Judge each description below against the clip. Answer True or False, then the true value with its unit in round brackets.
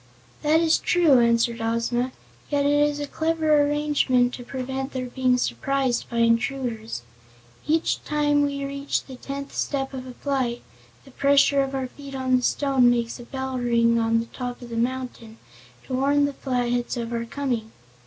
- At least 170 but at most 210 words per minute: True (175 wpm)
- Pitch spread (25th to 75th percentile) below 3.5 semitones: True (2.8 semitones)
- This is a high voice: True (260 Hz)